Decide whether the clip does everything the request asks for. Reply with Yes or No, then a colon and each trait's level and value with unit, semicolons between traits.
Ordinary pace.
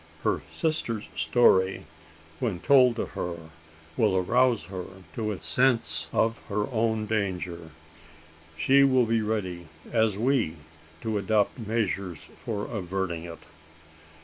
No: slow, 120 wpm